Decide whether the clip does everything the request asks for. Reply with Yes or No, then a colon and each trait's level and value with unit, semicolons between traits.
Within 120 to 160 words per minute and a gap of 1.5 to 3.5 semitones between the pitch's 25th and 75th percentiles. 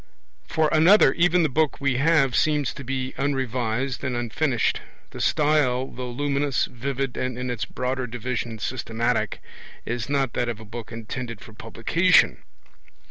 Yes: average, 150 wpm; average, 3.0 semitones